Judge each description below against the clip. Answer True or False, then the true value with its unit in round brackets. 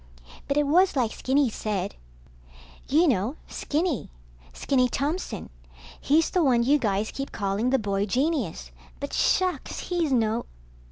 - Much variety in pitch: True (5.7 semitones)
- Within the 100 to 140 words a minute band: True (135 wpm)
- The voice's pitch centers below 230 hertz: False (260 Hz)